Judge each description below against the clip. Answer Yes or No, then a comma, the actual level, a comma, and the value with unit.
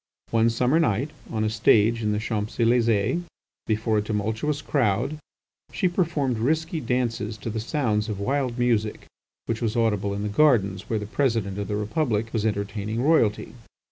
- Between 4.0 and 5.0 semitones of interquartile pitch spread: No, average, 3.3 semitones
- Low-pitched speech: Yes, low, 115 Hz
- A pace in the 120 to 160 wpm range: No, average, 170 wpm